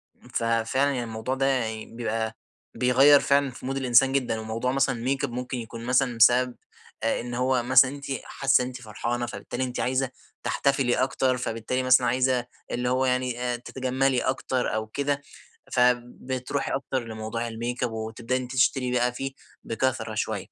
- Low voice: Yes, low, 125 Hz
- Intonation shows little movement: Yes, narrow, 1.8 semitones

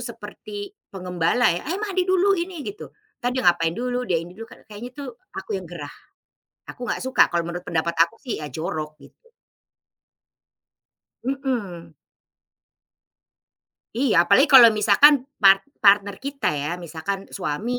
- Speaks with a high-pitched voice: Yes, high, 205 Hz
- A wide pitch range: Yes, wide, 7.5 semitones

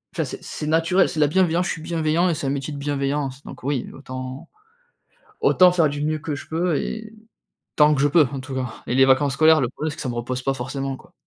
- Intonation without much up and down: No, average, 3.0 semitones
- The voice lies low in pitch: No, medium, 145 Hz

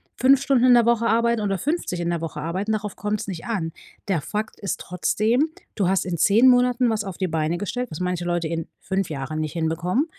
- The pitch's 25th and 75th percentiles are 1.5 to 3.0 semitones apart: No, wide, 5.5 semitones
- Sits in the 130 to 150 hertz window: No, high, 195 Hz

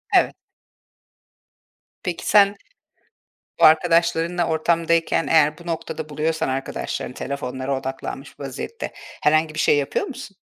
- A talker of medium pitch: Yes, medium, 160 Hz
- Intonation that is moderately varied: Yes, average, 3.1 semitones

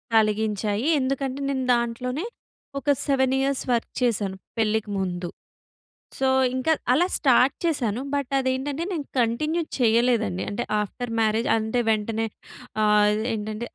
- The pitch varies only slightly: No, average, 3.8 semitones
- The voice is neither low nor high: No, high, 235 Hz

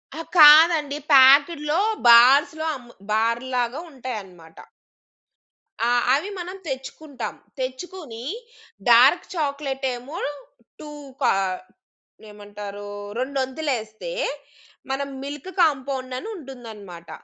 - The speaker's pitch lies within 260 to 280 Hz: Yes, very high, 265 Hz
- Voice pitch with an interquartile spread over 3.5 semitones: Yes, average, 4.0 semitones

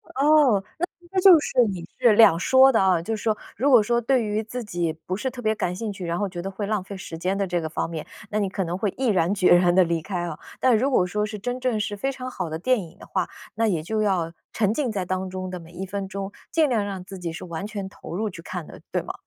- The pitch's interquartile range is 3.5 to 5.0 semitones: Yes, average, 4.1 semitones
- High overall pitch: Yes, high, 200 Hz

